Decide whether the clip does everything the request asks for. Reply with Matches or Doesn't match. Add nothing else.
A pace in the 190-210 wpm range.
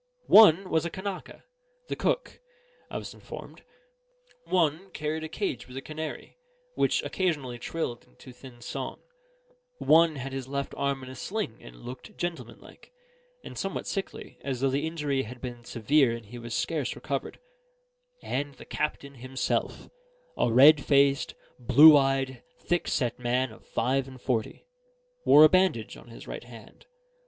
Doesn't match